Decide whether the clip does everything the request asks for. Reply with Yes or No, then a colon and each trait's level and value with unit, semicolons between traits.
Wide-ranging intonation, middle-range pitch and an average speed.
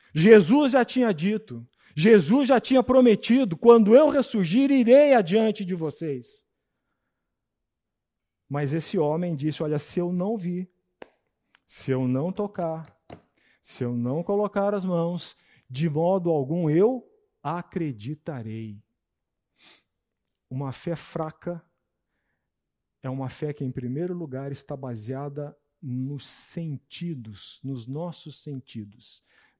No: wide, 7.3 semitones; medium, 165 Hz; slow, 115 wpm